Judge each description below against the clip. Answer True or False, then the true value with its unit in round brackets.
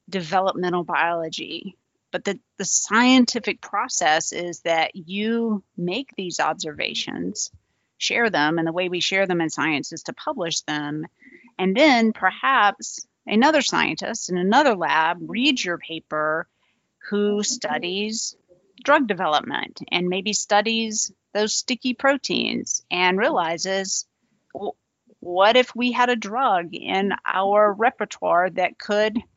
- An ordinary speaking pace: False (125 wpm)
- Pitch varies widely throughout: False (4.6 semitones)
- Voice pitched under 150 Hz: False (195 Hz)